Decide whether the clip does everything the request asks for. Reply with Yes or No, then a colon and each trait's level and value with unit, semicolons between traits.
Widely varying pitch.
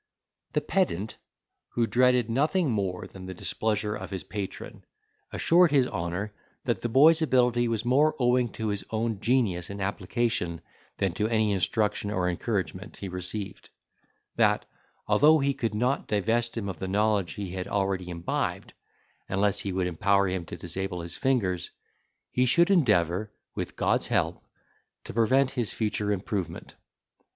No: average, 4.6 semitones